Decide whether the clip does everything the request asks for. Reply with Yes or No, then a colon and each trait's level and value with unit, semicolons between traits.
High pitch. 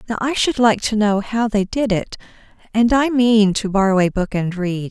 Yes: high, 210 Hz